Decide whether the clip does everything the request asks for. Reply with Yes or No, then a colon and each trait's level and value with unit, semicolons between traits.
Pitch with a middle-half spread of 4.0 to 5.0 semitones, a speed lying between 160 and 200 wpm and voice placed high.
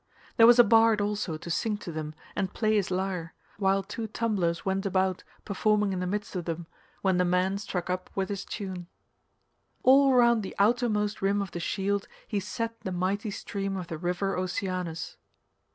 No: narrow, 2.4 semitones; average, 185 wpm; high, 195 Hz